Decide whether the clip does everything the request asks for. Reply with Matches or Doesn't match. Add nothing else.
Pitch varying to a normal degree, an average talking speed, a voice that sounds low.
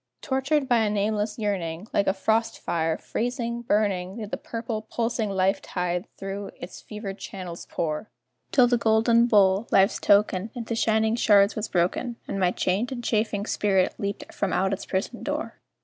Doesn't match